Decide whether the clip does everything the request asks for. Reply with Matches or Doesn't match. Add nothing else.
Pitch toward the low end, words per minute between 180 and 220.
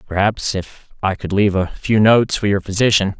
Matches